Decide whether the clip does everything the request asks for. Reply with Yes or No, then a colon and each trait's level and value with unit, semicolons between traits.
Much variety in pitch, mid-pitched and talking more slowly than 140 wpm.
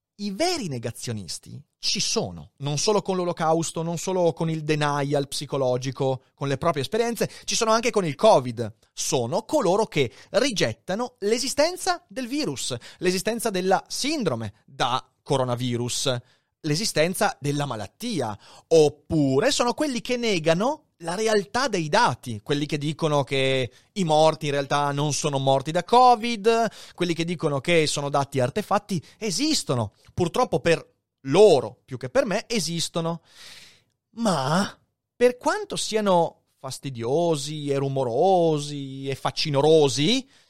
Yes: wide, 7.3 semitones; medium, 160 Hz; average, 130 wpm